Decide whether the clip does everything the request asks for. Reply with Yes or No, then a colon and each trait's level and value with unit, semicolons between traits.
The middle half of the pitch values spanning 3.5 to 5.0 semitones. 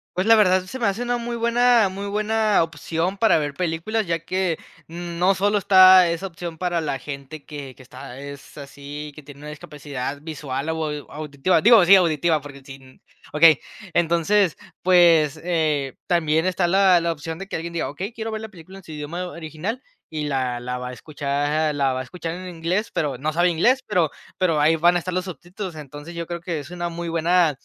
Yes: average, 3.8 semitones